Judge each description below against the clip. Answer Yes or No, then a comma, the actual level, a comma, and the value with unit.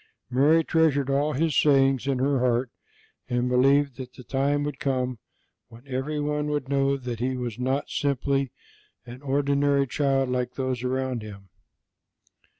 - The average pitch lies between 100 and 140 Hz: Yes, low, 135 Hz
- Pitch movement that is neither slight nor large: No, narrow, 2.0 semitones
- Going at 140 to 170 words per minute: Yes, average, 150 wpm